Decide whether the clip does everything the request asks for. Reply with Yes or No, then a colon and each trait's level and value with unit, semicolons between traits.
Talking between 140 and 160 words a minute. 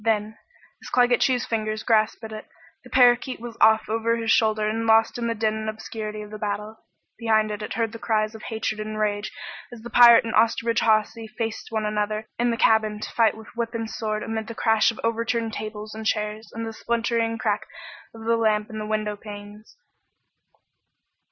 No: average, 200 wpm